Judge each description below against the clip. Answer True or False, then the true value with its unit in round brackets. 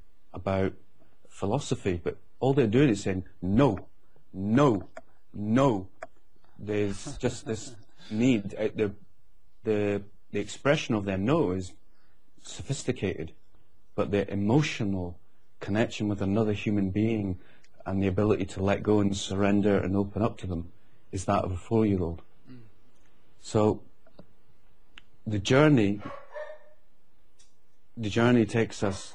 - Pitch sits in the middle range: False (105 Hz)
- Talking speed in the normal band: False (125 wpm)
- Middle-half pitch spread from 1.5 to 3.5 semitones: True (2.9 semitones)